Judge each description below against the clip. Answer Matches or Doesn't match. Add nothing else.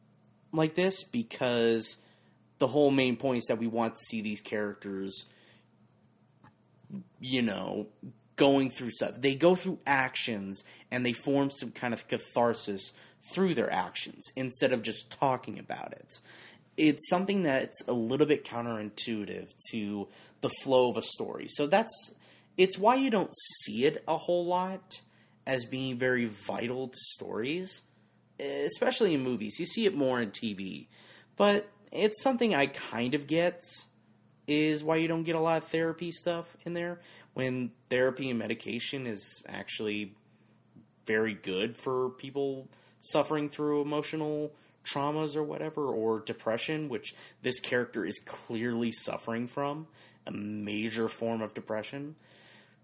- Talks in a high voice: Doesn't match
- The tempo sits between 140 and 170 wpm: Matches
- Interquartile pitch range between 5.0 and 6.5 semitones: Matches